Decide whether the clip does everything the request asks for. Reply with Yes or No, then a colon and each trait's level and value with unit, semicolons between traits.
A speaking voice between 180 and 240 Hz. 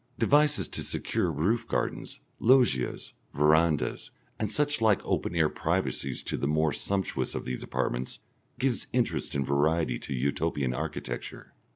No: very low, 80 Hz